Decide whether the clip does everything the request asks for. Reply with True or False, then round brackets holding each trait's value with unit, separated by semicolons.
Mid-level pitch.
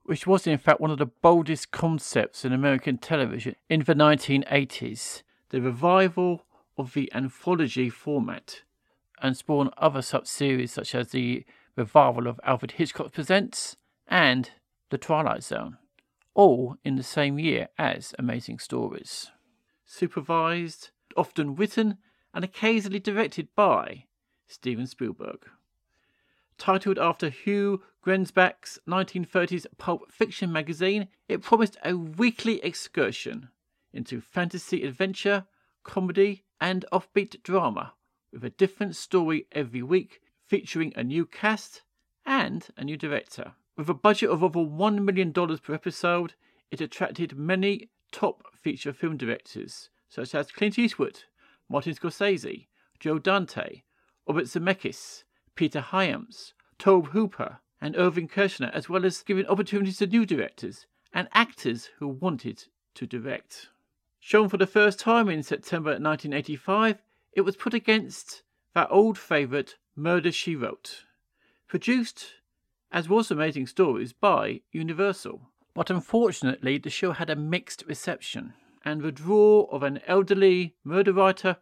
True (175 Hz)